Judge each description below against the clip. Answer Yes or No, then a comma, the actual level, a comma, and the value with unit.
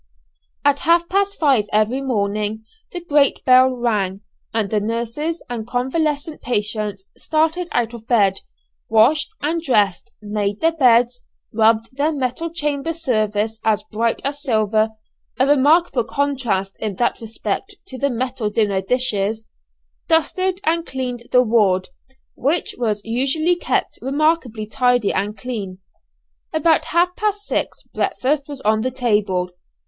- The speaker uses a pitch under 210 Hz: No, high, 245 Hz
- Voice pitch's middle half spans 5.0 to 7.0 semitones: Yes, wide, 5.5 semitones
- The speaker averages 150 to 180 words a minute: No, slow, 135 wpm